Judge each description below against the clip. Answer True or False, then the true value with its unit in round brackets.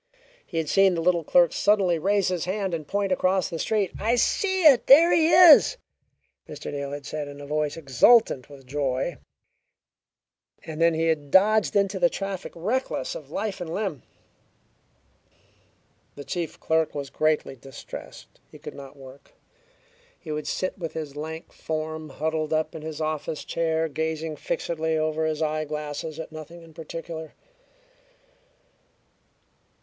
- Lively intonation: False (3.7 semitones)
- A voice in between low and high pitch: True (160 Hz)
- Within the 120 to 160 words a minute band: True (155 wpm)